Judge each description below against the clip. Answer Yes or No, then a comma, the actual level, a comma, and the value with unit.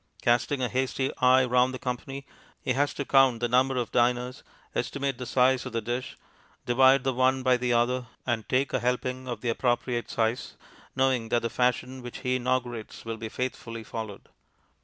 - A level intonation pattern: Yes, narrow, 1.4 semitones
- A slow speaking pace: No, average, 185 wpm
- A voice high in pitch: No, low, 125 Hz